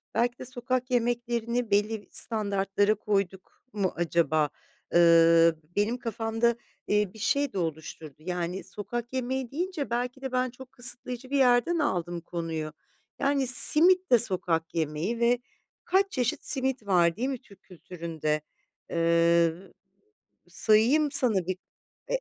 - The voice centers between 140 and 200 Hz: No, high, 220 Hz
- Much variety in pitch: Yes, wide, 6.4 semitones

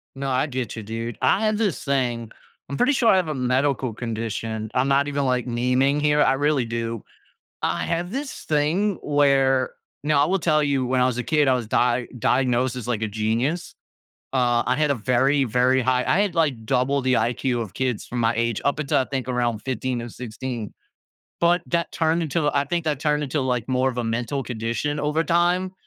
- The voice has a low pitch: Yes, low, 130 Hz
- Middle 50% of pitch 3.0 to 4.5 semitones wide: Yes, average, 3.7 semitones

